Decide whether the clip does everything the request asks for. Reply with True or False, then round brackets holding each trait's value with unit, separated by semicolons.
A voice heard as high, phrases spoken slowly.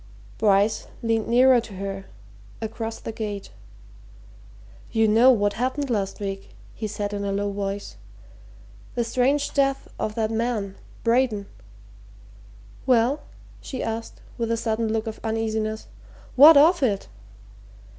True (225 Hz; 130 wpm)